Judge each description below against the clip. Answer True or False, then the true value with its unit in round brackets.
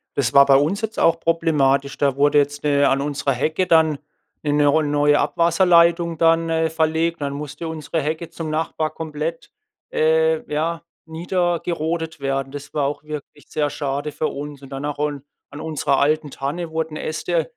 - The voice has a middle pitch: True (155 Hz)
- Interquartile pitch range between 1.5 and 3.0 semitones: True (2.4 semitones)